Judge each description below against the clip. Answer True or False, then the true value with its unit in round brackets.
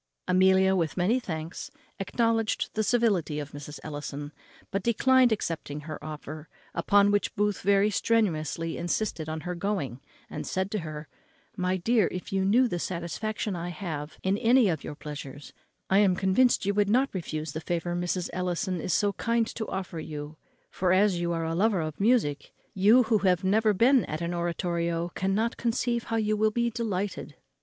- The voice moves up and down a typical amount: True (4.6 semitones)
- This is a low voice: False (185 Hz)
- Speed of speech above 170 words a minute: True (180 wpm)